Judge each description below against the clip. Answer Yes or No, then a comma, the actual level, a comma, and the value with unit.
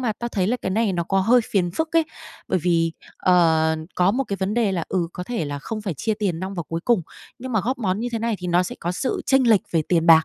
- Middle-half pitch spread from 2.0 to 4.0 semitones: No, average, 4.9 semitones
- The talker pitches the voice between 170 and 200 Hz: Yes, high, 190 Hz